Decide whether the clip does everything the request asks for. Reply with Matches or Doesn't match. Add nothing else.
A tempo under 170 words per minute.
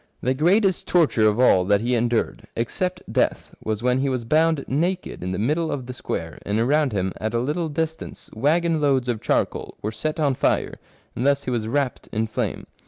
Doesn't match